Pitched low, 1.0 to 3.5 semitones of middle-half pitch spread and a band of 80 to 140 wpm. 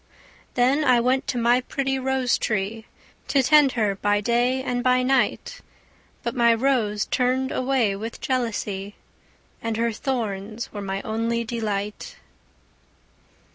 No: high, 235 Hz; average, 3.2 semitones; slow, 135 wpm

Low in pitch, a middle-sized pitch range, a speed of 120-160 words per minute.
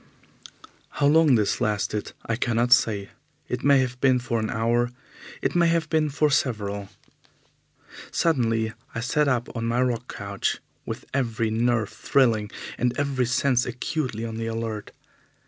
Yes: low, 120 Hz; average, 3.0 semitones; average, 150 wpm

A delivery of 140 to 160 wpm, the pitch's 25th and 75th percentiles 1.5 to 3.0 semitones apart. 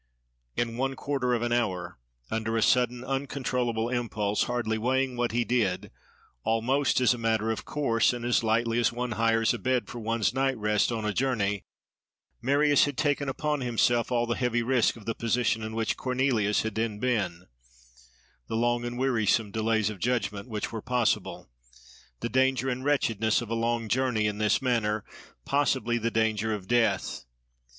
No: average, 175 wpm; narrow, 2.4 semitones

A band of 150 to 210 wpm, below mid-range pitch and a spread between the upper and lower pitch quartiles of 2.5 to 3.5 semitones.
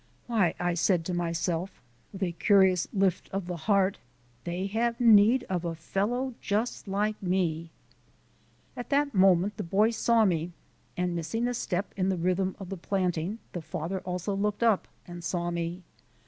No: average, 170 wpm; high, 190 Hz; average, 3.2 semitones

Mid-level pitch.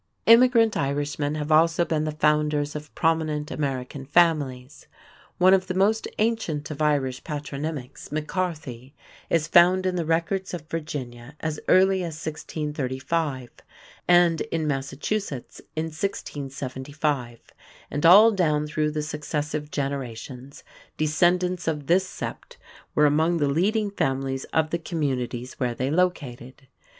Yes: medium, 150 Hz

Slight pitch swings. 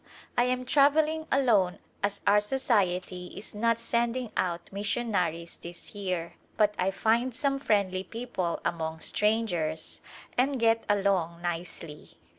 No: average, 5.1 semitones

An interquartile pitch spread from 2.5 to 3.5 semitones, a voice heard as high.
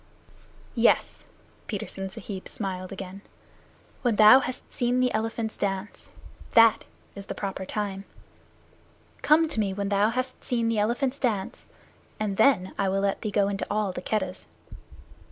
Yes: average, 2.8 semitones; high, 210 Hz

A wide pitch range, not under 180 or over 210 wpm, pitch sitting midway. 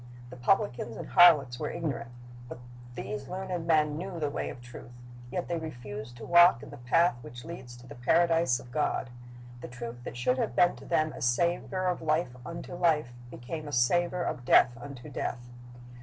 Yes: wide, 5.8 semitones; average, 195 wpm; medium, 145 Hz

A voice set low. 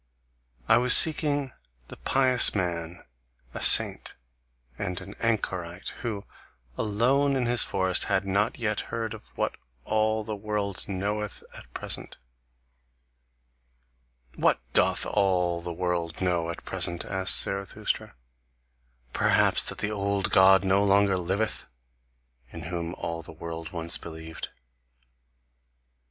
Yes: very low, 95 Hz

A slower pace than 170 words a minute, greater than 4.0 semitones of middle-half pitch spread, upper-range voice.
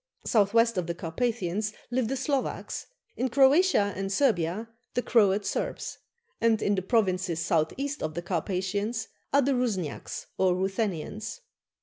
Yes: average, 145 wpm; average, 4.8 semitones; high, 205 Hz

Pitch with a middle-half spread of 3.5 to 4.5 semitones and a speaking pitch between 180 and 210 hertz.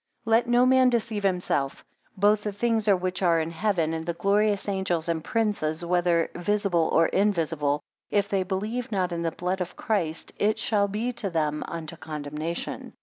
Yes: average, 4.1 semitones; medium, 185 Hz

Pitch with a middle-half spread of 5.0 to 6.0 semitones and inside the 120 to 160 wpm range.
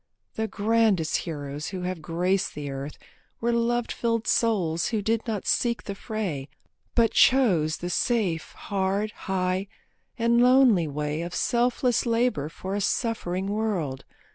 Yes: wide, 5.6 semitones; average, 140 wpm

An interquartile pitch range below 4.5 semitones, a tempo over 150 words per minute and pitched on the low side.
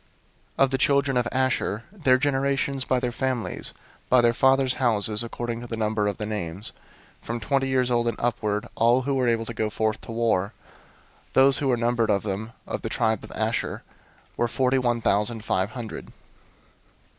Yes: average, 3.0 semitones; average, 190 wpm; low, 120 Hz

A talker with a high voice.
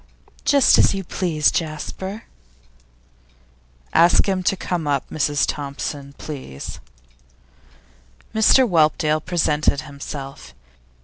No: medium, 155 Hz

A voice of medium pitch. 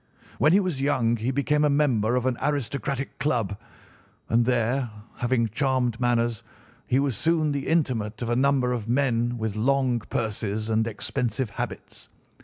No: low, 125 Hz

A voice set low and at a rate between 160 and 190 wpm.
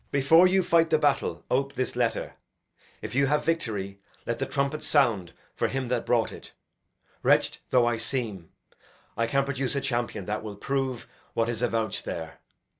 Yes: low, 125 Hz; average, 175 wpm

